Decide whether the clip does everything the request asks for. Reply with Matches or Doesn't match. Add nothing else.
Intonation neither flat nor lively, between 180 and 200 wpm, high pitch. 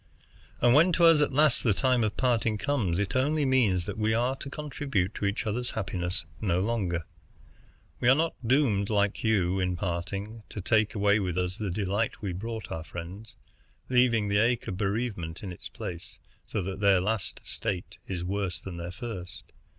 Doesn't match